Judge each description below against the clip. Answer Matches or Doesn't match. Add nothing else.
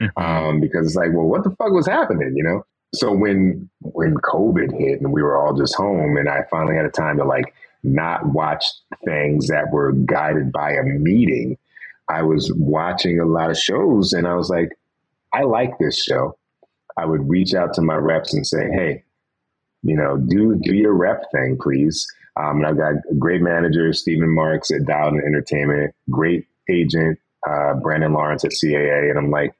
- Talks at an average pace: Matches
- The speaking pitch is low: Matches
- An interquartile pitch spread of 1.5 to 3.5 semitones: Matches